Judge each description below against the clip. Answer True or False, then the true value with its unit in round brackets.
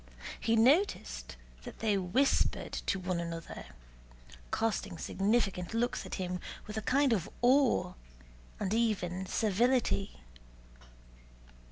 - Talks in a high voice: True (210 Hz)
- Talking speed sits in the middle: False (110 wpm)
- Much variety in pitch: False (4.6 semitones)